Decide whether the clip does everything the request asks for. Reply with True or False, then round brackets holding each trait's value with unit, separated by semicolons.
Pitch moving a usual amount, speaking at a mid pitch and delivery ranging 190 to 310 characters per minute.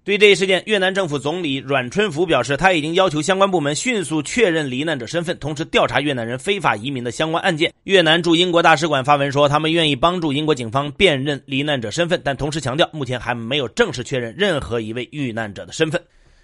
False (4.4 semitones; 150 Hz; 370 characters per minute)